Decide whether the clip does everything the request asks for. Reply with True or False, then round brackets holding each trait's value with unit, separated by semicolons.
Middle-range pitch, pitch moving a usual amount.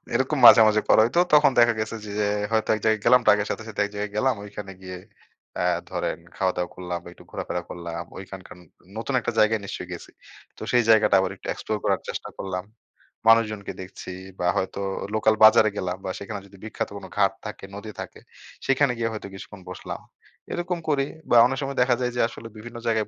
False (105 Hz; 3.1 semitones)